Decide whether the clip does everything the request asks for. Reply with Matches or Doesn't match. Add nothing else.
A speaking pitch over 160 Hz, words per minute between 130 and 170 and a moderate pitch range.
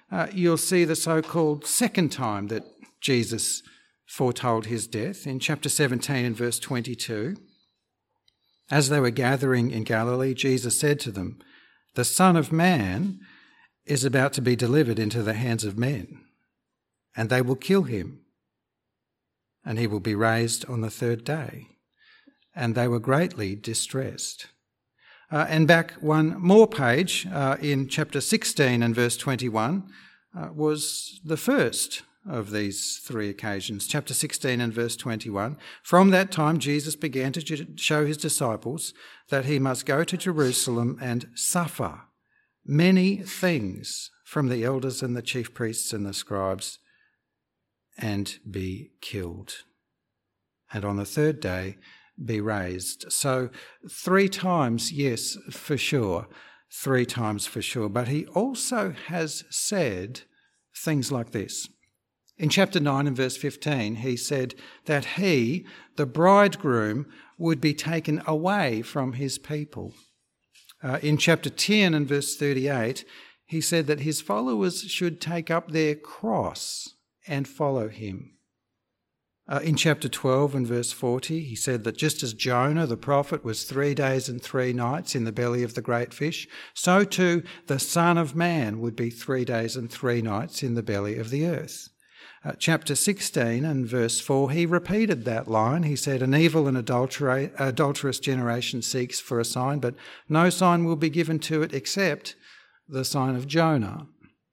Doesn't match